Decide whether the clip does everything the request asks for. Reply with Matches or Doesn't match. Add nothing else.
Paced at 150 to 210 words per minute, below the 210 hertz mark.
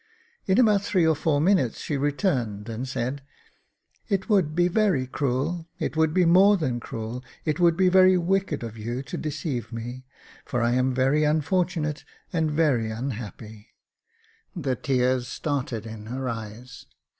Matches